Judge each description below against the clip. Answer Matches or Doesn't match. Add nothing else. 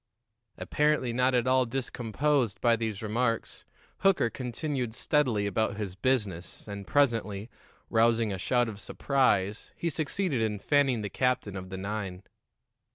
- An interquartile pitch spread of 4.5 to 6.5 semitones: Doesn't match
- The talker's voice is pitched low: Matches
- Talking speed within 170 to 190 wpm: Doesn't match